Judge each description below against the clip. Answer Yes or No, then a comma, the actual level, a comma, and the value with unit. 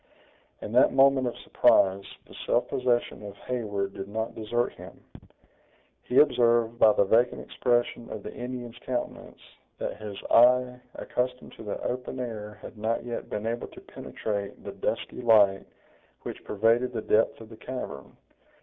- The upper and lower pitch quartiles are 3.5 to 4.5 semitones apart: No, average, 2.8 semitones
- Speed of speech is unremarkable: Yes, average, 160 wpm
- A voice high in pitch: No, low, 115 Hz